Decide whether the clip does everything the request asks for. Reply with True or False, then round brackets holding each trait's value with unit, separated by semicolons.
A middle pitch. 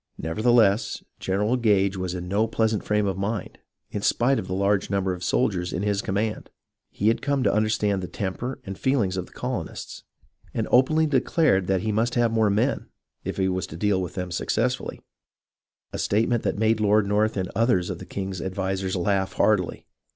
False (100 Hz)